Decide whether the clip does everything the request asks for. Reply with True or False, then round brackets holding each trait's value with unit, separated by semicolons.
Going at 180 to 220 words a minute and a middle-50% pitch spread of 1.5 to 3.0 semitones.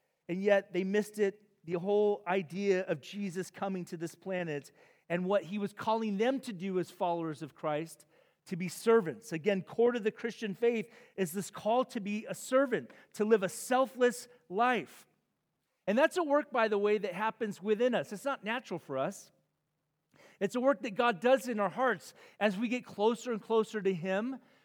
False (195 wpm; 4.3 semitones)